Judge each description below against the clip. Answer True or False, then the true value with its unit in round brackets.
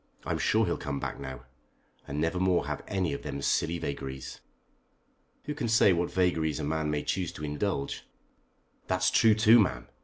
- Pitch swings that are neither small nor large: True (4.6 semitones)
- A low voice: True (80 Hz)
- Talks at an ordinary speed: True (180 wpm)